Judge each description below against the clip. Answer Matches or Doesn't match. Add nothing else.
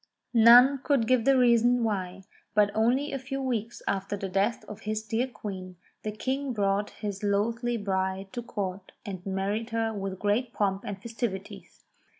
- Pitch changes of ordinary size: Matches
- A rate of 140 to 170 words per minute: Matches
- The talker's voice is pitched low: Doesn't match